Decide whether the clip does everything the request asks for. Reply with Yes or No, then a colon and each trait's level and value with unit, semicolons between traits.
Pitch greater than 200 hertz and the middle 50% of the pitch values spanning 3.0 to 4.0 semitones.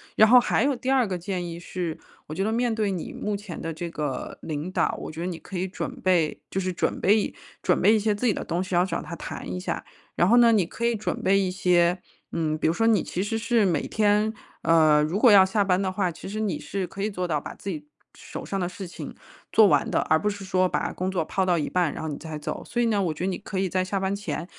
No: medium, 185 Hz; average, 3.4 semitones